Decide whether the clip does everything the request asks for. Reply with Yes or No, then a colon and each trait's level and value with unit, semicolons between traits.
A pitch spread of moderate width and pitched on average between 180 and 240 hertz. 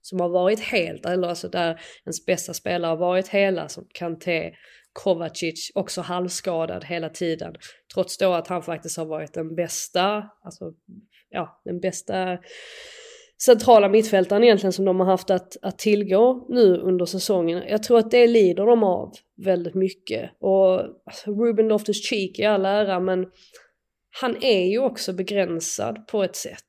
Yes: average, 3.1 semitones; high, 190 Hz